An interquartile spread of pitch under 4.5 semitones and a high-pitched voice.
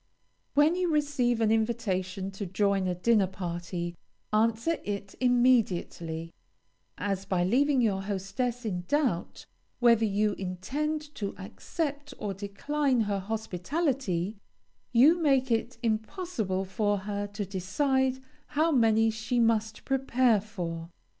No: average, 5.0 semitones; high, 220 Hz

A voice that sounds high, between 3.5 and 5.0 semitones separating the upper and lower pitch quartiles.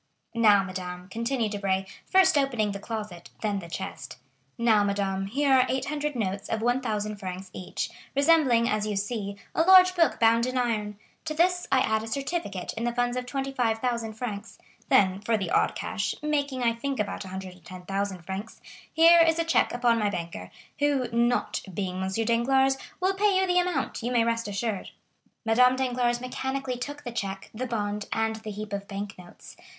Yes: high, 230 Hz; average, 4.6 semitones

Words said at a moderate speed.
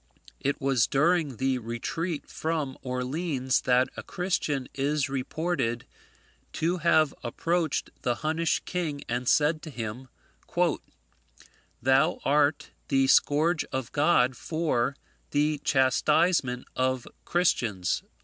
No: slow, 110 wpm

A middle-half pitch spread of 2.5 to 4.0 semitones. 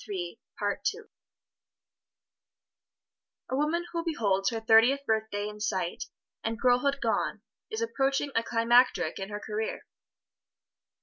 No: average, 4.8 semitones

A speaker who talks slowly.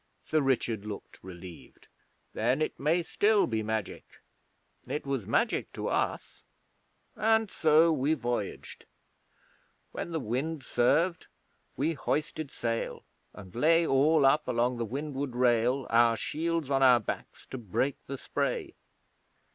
Yes: slow, 130 wpm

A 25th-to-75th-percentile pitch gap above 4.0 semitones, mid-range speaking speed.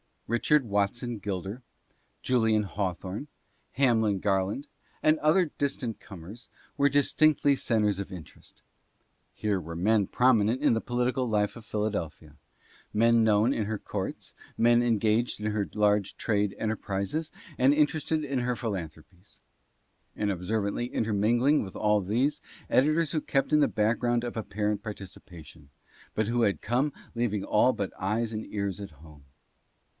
No: average, 3.5 semitones; average, 150 wpm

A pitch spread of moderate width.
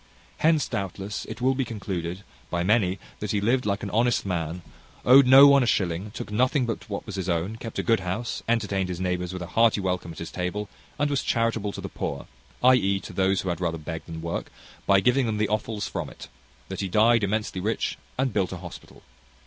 Yes: average, 4.2 semitones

